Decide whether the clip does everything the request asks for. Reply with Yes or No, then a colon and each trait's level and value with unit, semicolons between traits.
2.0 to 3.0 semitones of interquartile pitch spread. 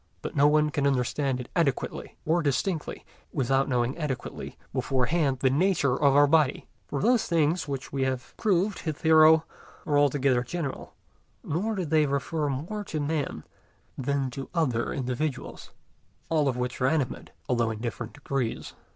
No: average, 3.4 semitones